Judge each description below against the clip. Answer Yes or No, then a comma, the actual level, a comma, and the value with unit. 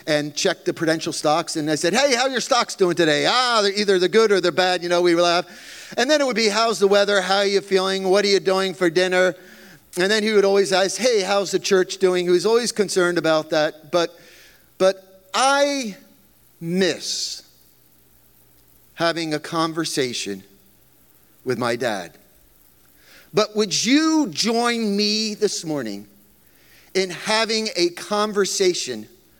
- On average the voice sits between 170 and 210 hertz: Yes, high, 190 Hz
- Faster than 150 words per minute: Yes, average, 170 wpm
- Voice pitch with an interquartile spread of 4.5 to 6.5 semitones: No, average, 3.9 semitones